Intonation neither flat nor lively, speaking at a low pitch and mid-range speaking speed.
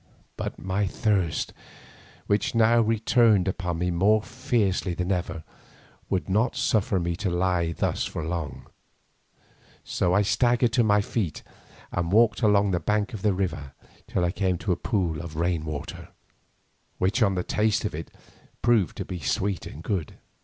Yes: average, 3.6 semitones; very low, 95 Hz; average, 160 wpm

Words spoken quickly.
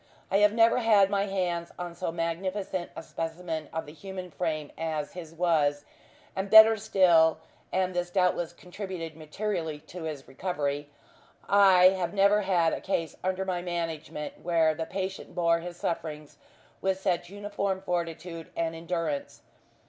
No: average, 150 wpm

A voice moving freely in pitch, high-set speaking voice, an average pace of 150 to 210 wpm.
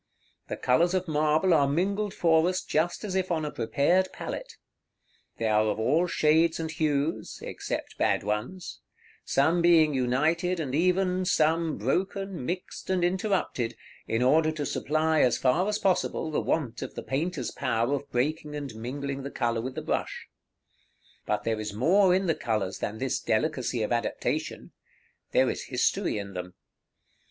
No: wide, 5.9 semitones; medium, 155 Hz; average, 165 wpm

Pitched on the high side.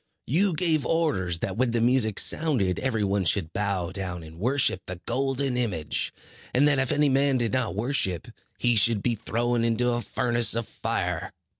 No: low, 120 Hz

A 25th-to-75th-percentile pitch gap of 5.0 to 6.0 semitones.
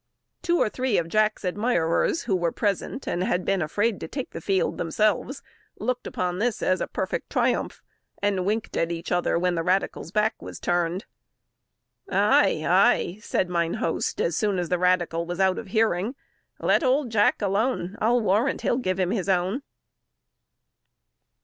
No: average, 3.9 semitones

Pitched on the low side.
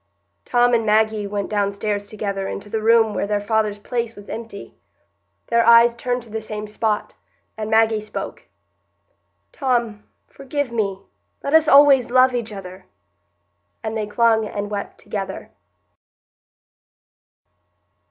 No: high, 220 Hz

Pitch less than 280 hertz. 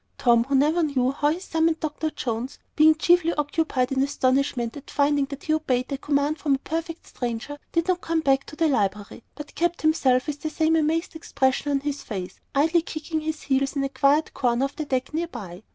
No: very high, 290 Hz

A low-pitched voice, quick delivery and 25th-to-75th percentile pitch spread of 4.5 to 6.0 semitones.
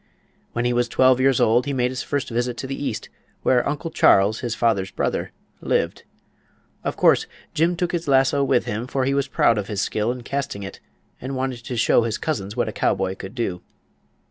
No: low, 125 Hz; fast, 210 wpm; average, 3.3 semitones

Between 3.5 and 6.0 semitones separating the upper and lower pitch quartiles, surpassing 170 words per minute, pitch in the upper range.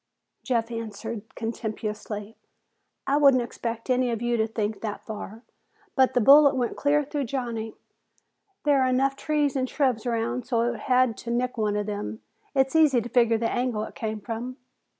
No: narrow, 2.6 semitones; average, 180 wpm; high, 240 Hz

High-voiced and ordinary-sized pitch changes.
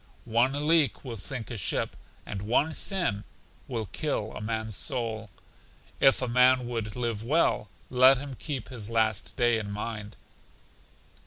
No: low, 120 Hz; average, 3.1 semitones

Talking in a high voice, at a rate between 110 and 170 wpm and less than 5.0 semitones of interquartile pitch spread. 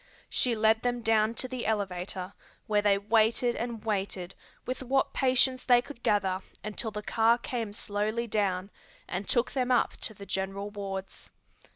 Yes: high, 220 Hz; average, 165 wpm; average, 3.1 semitones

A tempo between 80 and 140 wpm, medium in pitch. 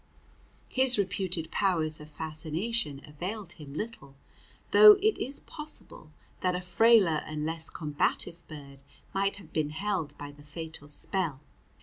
Yes: slow, 135 wpm; medium, 165 Hz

